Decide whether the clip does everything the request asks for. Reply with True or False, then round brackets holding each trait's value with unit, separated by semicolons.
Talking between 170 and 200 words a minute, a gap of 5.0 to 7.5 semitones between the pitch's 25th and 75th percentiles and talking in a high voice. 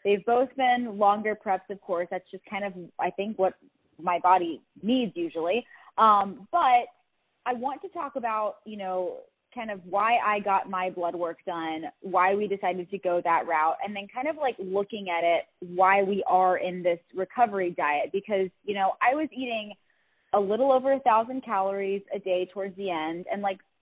False (195 wpm; 3.8 semitones; 195 Hz)